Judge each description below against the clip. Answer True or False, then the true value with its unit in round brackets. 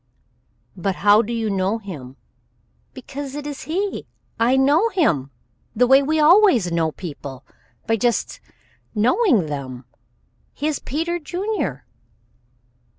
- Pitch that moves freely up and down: True (8.8 semitones)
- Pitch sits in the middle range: False (240 Hz)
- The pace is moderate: False (125 wpm)